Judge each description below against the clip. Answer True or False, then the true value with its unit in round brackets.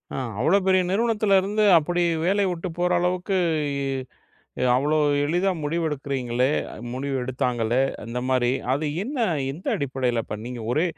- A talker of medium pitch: True (150 Hz)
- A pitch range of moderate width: False (6.3 semitones)